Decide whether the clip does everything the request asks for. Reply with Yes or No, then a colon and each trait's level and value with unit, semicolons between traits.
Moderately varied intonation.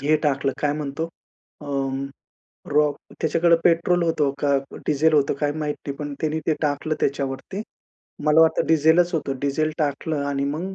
No: narrow, 2.1 semitones